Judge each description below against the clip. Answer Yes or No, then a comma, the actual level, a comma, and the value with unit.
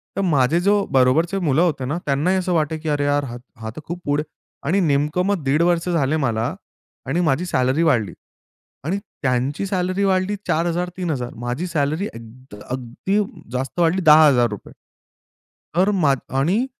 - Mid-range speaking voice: Yes, medium, 155 Hz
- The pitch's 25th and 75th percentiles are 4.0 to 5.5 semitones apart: Yes, average, 5.1 semitones